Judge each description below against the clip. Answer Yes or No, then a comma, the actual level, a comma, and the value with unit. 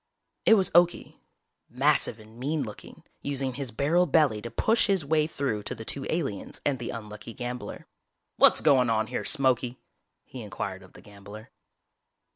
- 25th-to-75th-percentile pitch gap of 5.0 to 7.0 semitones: Yes, average, 5.3 semitones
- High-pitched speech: No, low, 130 Hz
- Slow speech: No, average, 165 wpm